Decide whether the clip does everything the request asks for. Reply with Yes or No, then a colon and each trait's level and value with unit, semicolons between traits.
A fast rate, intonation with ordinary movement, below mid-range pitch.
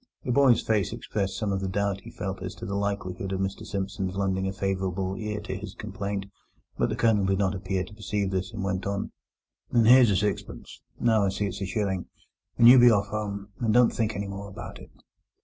No: fast, 220 wpm; narrow, 1.8 semitones; low, 100 Hz